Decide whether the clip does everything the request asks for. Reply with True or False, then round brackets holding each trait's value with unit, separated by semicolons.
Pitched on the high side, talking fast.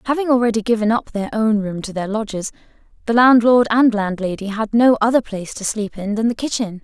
True (220 Hz; 210 wpm)